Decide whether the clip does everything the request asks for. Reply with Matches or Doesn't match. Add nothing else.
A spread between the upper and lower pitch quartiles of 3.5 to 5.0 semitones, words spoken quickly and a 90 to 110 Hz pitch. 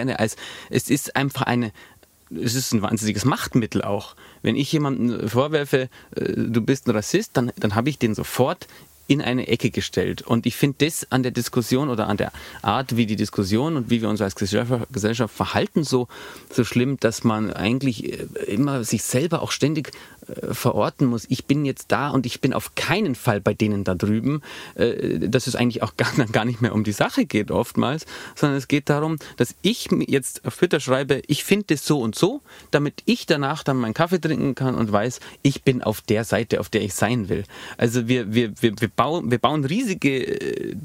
Doesn't match